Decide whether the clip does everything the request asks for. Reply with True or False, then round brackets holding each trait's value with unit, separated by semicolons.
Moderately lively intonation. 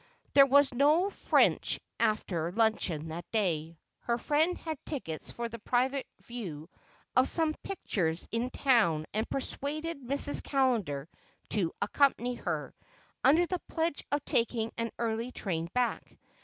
False (6.6 semitones)